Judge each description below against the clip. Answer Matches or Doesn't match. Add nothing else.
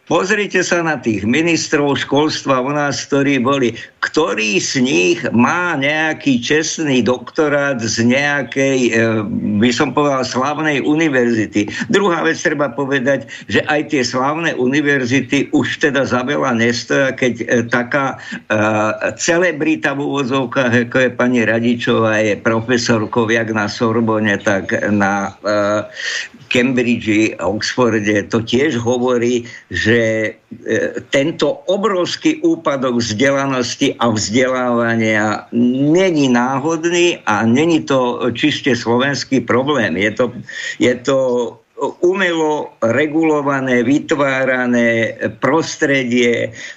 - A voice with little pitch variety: Doesn't match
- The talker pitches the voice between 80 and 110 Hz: Doesn't match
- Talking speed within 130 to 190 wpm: Doesn't match